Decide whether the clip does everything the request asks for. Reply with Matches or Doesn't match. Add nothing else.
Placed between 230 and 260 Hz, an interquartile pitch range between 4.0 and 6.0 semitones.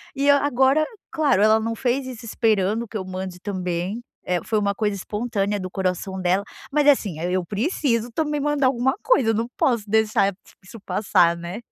Doesn't match